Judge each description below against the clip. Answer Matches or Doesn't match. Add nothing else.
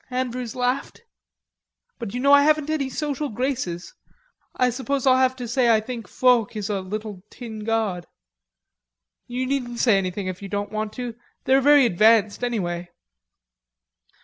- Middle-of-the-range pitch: Doesn't match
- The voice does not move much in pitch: Doesn't match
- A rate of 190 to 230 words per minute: Doesn't match